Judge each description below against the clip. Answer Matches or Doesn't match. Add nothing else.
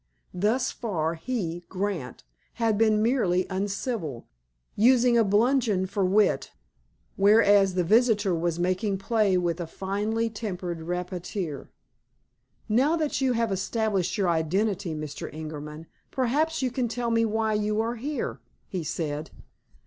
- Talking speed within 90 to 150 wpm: Matches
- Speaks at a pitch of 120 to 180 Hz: Doesn't match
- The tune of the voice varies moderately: Matches